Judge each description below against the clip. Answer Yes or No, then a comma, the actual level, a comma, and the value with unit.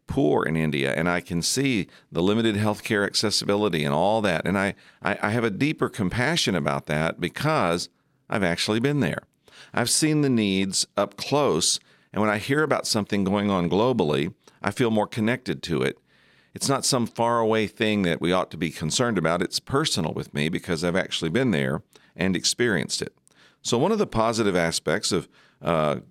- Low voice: Yes, low, 105 Hz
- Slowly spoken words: No, average, 190 wpm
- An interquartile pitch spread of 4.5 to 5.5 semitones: Yes, average, 5.1 semitones